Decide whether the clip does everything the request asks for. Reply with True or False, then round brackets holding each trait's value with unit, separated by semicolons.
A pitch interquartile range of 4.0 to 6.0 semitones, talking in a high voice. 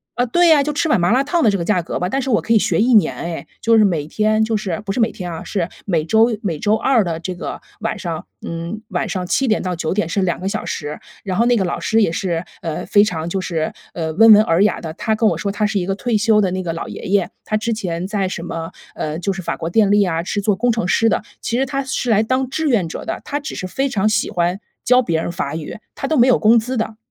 True (4.6 semitones; 205 Hz)